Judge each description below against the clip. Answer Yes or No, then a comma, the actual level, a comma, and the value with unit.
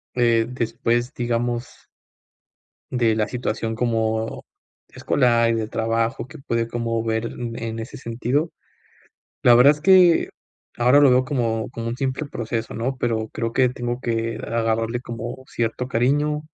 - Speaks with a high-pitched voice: No, low, 120 Hz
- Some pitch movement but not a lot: No, narrow, 1.8 semitones